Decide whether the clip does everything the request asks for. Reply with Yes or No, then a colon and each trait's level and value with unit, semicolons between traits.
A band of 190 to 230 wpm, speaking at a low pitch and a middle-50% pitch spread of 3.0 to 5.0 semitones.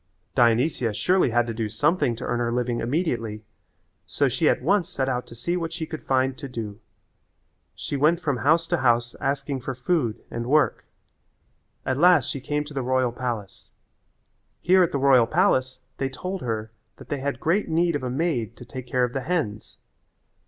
Yes: average, 195 wpm; low, 130 Hz; average, 4.7 semitones